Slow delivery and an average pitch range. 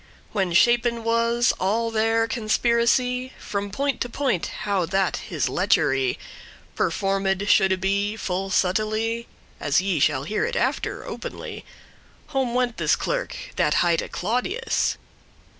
Yes: slow, 130 wpm; average, 3.8 semitones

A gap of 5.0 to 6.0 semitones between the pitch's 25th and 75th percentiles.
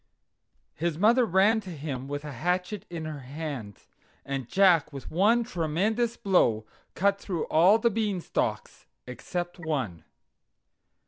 Yes: wide, 5.6 semitones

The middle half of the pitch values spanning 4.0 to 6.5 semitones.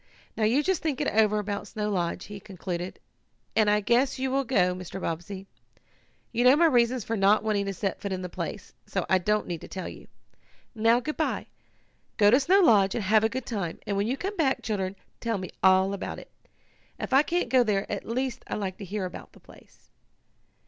Yes: average, 4.5 semitones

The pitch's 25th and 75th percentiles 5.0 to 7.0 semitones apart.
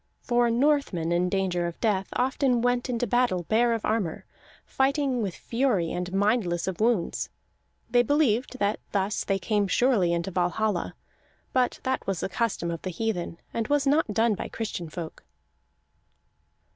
Yes: average, 5.3 semitones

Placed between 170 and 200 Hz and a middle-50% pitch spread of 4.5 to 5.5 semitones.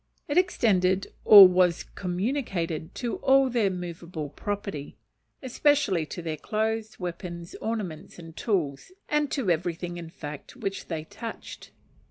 Yes: medium, 185 Hz; average, 4.8 semitones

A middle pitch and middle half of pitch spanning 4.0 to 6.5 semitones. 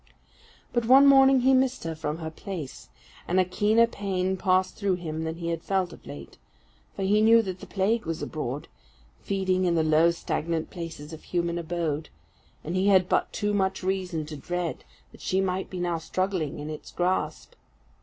No: medium, 180 Hz; average, 3.1 semitones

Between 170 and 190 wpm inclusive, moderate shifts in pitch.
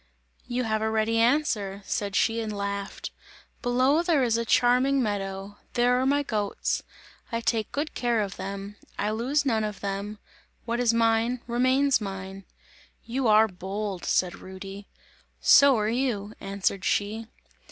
No: average, 150 wpm; average, 3.5 semitones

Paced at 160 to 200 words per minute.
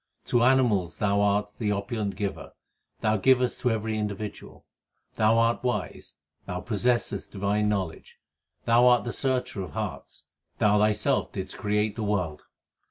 No: average, 150 wpm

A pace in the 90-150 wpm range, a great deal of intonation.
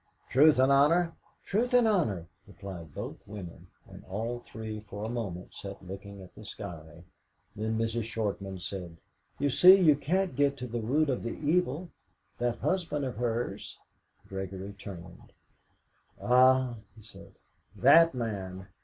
Yes: average, 145 wpm; wide, 6.5 semitones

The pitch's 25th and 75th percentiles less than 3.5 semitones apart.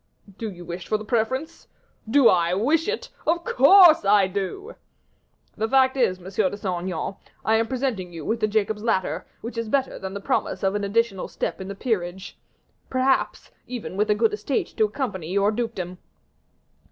No: average, 4.7 semitones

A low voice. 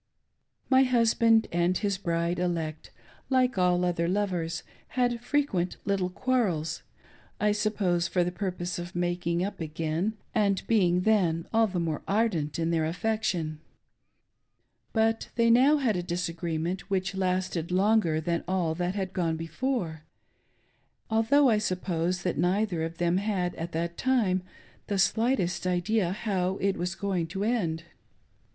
No: medium, 185 Hz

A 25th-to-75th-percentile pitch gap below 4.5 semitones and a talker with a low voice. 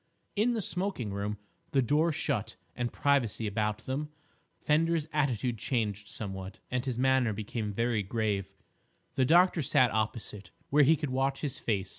No: wide, 5.5 semitones; low, 120 Hz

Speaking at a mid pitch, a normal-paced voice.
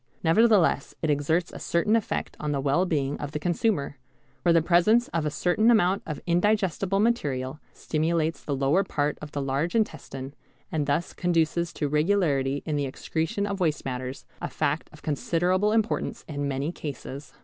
Yes: medium, 160 Hz; average, 170 wpm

